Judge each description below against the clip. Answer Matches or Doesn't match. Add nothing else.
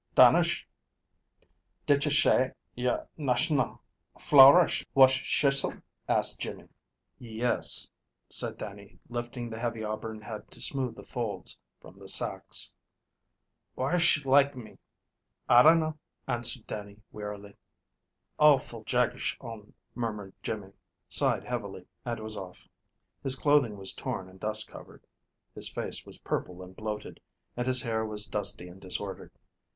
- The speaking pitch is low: Matches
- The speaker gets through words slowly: Matches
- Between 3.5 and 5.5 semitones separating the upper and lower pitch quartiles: Matches